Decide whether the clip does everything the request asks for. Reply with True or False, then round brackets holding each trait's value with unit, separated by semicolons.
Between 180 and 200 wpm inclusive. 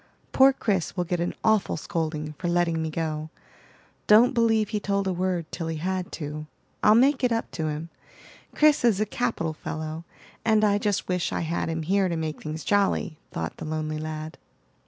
True (195 wpm)